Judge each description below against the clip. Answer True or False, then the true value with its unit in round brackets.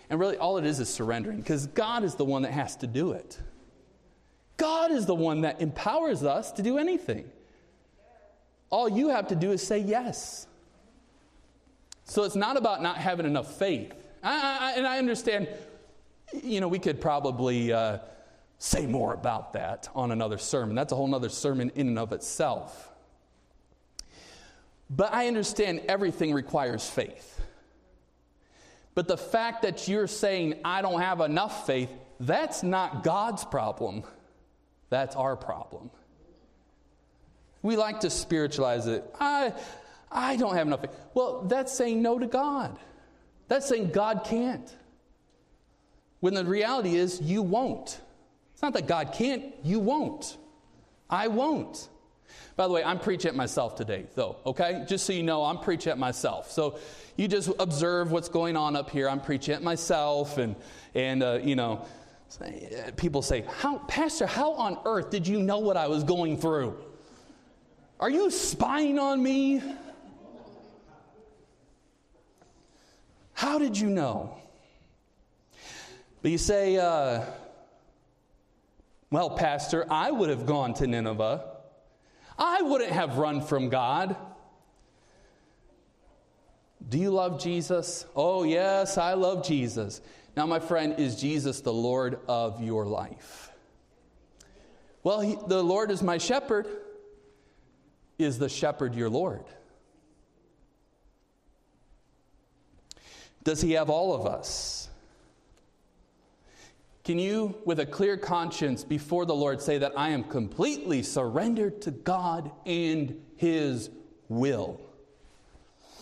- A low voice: False (170 Hz)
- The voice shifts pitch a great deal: True (7.3 semitones)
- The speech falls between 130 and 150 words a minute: True (145 wpm)